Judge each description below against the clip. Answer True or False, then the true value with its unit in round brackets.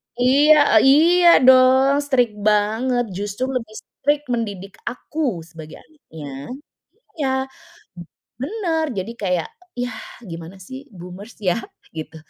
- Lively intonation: True (6.3 semitones)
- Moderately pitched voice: False (240 Hz)